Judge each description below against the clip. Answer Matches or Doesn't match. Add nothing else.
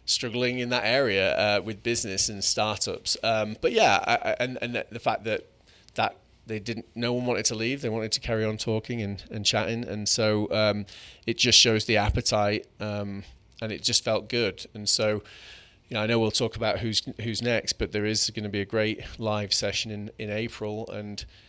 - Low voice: Matches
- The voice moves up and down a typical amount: Doesn't match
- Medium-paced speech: Doesn't match